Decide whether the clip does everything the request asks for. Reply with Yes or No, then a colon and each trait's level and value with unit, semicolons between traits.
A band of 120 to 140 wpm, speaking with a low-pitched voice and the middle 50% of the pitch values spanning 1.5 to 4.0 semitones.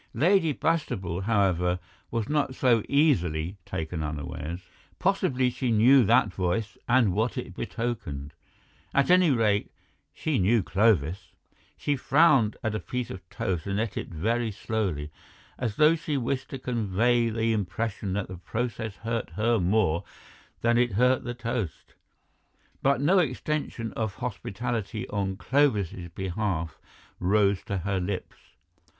No: slow, 135 wpm; low, 110 Hz; average, 4.7 semitones